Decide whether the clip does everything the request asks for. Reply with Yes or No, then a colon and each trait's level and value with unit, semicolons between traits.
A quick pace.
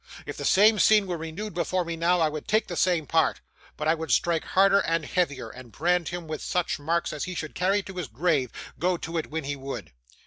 Yes: fast, 240 wpm